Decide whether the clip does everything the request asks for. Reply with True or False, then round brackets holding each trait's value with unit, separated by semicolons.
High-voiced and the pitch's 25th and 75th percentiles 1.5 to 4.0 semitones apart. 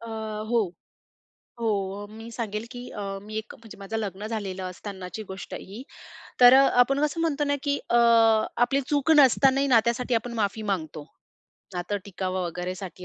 False (225 Hz; 4.8 semitones)